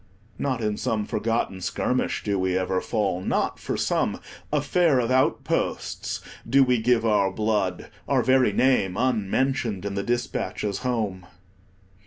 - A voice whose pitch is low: Yes, low, 110 Hz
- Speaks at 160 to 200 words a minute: No, average, 140 wpm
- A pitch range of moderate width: Yes, average, 4.4 semitones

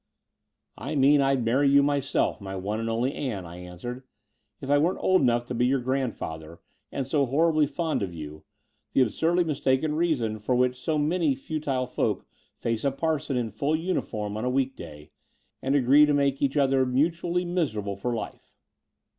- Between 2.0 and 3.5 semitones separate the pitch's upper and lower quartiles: No, average, 4.4 semitones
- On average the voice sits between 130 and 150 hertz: Yes, low, 135 Hz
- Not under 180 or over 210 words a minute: Yes, average, 190 wpm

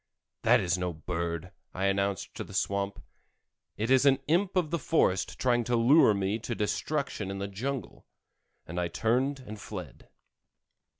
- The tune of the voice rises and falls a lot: Yes, wide, 5.7 semitones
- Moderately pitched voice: No, low, 105 Hz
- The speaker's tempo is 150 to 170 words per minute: Yes, average, 165 wpm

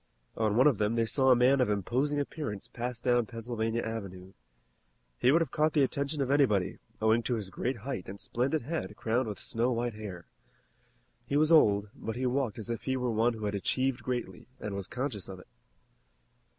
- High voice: No, low, 120 Hz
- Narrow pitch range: No, average, 3.7 semitones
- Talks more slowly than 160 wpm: No, fast, 205 wpm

